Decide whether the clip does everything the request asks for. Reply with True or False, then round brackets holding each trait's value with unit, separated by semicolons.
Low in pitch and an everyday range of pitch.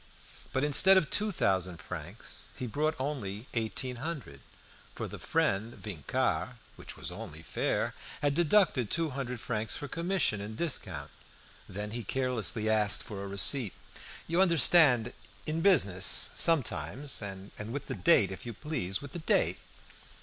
False (125 Hz; 7.0 semitones)